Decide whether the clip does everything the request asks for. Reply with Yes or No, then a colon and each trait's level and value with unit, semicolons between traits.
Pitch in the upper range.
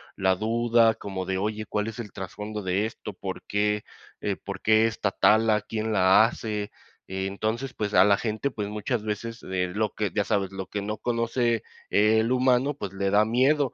No: low, 105 Hz